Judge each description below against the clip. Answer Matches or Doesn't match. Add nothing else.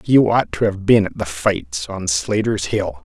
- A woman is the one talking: Doesn't match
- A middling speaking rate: Doesn't match